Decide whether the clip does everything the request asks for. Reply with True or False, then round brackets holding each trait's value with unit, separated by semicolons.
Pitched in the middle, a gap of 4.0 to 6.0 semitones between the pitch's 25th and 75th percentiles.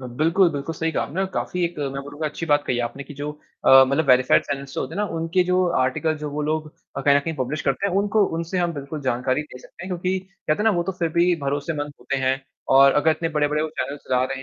False (150 Hz; 3.5 semitones)